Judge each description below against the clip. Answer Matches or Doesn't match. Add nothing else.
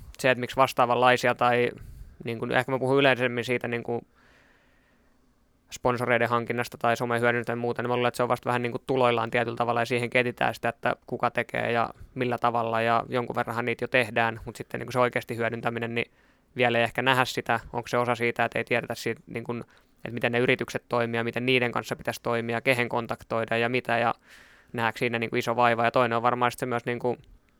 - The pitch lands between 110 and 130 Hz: Matches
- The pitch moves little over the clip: Matches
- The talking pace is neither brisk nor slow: Doesn't match